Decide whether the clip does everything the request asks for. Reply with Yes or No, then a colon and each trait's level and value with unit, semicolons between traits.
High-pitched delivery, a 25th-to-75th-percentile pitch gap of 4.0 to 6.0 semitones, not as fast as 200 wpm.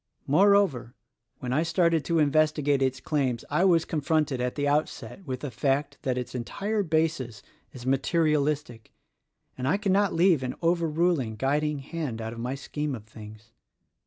No: medium, 145 Hz; average, 4.4 semitones; average, 160 wpm